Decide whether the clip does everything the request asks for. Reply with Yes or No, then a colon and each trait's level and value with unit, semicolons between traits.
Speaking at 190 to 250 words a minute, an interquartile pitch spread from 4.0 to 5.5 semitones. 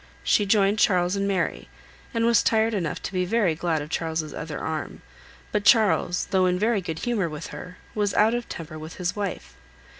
Yes: average, 200 wpm; average, 4.3 semitones